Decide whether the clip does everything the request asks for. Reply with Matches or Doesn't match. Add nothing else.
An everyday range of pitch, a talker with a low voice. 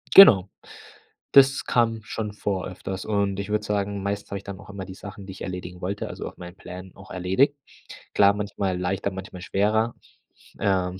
Doesn't match